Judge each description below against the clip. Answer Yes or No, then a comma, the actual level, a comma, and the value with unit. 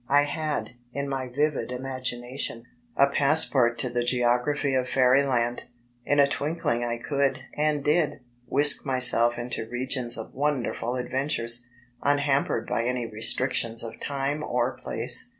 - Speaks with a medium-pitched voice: No, low, 130 Hz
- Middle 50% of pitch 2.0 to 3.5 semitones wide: Yes, average, 2.9 semitones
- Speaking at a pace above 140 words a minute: No, slow, 135 wpm